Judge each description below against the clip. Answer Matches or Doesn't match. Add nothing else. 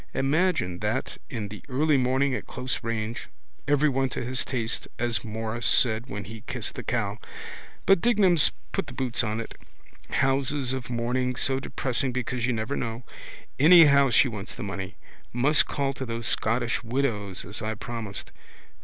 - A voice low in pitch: Matches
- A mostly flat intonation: Doesn't match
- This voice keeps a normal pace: Matches